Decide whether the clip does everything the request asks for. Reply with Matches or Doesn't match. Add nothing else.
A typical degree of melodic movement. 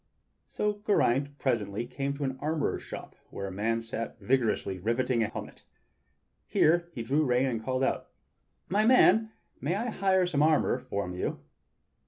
Doesn't match